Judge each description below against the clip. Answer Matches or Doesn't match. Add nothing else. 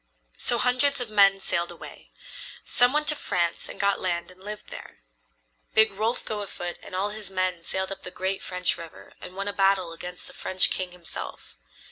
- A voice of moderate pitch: Doesn't match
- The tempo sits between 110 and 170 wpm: Doesn't match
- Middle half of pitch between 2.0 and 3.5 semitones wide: Matches